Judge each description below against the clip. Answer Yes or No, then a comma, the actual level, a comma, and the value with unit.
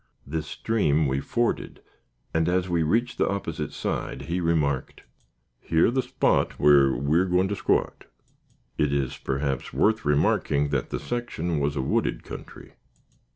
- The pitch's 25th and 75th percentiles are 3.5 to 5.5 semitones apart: Yes, average, 4.6 semitones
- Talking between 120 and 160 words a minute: Yes, average, 150 wpm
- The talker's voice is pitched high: No, very low, 80 Hz